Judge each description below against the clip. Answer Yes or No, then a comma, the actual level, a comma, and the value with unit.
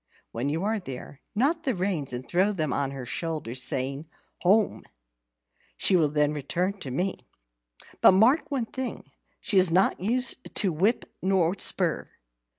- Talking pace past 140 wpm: Yes, average, 155 wpm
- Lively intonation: Yes, wide, 6.3 semitones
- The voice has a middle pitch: Yes, medium, 180 Hz